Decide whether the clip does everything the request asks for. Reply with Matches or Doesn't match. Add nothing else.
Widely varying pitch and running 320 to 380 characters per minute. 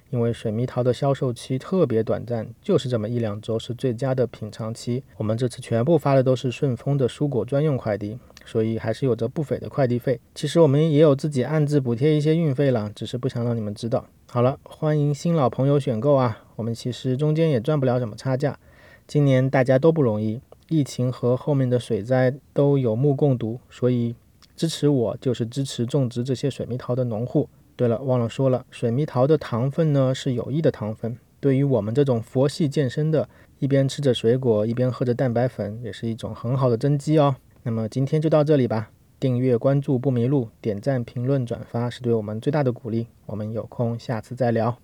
Doesn't match